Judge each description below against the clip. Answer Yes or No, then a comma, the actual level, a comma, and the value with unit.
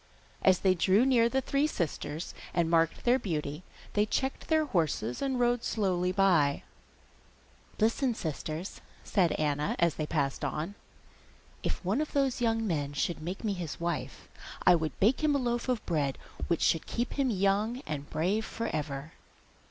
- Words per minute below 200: Yes, average, 165 wpm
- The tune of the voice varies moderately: No, wide, 7.2 semitones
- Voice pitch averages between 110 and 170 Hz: No, medium, 185 Hz